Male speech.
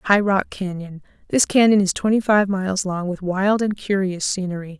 No: female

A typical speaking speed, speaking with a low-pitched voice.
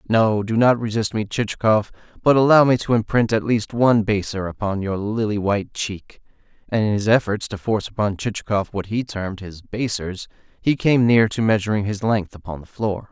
Yes: average, 195 wpm; low, 105 Hz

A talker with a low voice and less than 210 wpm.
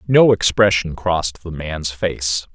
Yes: very low, 85 Hz; average, 140 wpm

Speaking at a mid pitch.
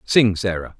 No: very low, 95 Hz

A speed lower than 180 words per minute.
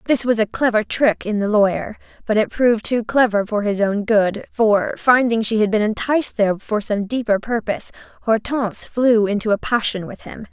No: average, 200 wpm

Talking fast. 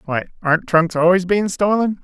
No: average, 175 wpm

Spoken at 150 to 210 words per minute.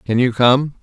No: fast, 220 wpm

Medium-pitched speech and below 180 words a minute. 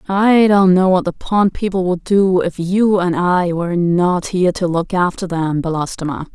No: medium, 180 Hz; average, 200 wpm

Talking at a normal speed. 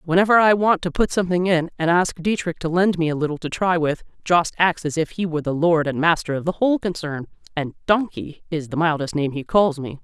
No: fast, 245 wpm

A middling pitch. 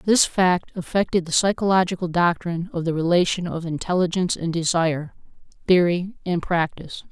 Yes: medium, 175 Hz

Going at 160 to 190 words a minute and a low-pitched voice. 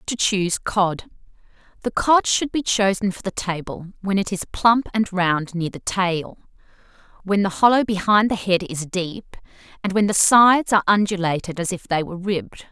No: average, 180 wpm; high, 195 Hz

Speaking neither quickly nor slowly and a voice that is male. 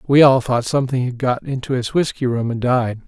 No: fast, 235 wpm; male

